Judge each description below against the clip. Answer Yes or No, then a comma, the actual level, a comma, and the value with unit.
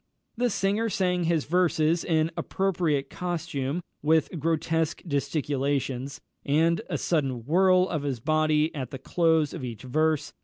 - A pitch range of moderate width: Yes, average, 3.5 semitones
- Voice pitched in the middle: Yes, medium, 155 Hz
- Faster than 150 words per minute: No, average, 140 wpm